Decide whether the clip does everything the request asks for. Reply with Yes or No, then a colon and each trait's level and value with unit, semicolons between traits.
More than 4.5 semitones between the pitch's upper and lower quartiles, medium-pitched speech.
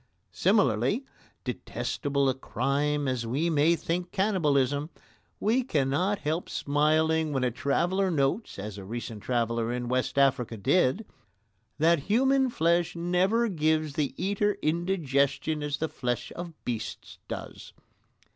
Yes: average, 5.0 semitones; medium, 150 Hz